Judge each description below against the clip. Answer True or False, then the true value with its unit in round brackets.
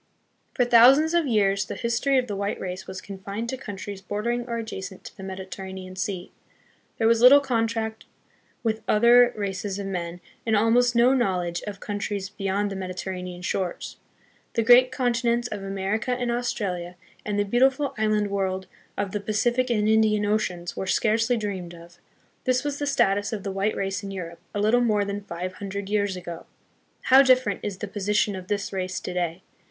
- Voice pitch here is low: False (205 Hz)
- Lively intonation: False (3.6 semitones)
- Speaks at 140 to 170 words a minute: False (185 wpm)